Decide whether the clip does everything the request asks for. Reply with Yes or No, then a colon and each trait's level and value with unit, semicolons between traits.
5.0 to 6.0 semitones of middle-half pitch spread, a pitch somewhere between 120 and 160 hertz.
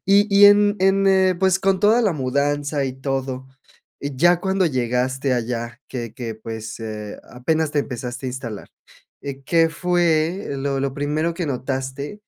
Yes: wide, 5.5 semitones; medium, 140 Hz